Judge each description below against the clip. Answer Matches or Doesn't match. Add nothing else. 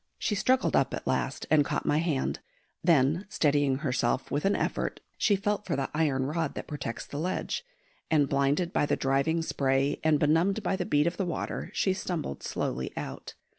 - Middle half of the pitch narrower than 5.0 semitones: Matches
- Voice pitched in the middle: Matches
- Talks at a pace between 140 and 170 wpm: Doesn't match